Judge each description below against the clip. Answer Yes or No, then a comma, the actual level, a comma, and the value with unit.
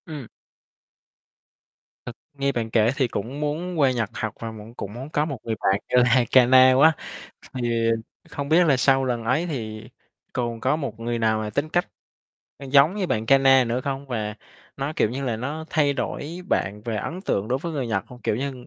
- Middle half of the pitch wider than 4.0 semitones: No, average, 3.7 semitones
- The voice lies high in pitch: No, low, 130 Hz